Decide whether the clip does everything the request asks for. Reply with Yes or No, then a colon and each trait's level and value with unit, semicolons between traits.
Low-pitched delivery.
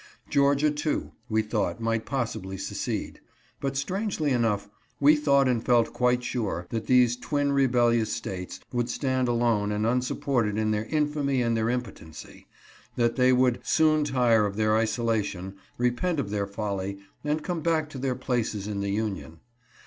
Yes: low, 120 Hz